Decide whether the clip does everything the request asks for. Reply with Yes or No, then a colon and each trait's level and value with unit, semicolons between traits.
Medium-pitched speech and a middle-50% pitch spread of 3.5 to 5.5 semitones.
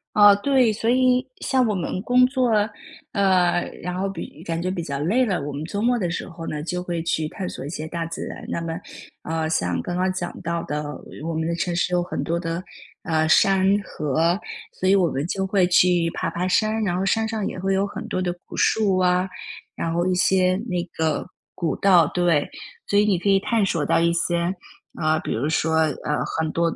No: medium, 180 Hz; average, 2.9 semitones